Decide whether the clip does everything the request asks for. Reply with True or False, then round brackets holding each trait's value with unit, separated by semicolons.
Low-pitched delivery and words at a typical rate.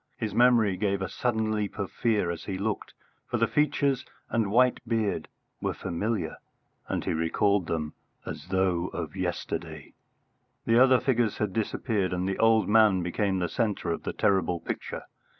True (100 Hz; 170 wpm)